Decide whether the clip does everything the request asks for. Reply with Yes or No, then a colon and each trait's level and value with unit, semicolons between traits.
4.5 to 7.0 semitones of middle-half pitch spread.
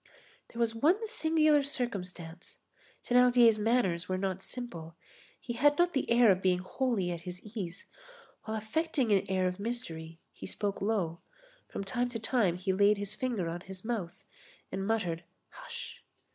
Yes: average, 5.2 semitones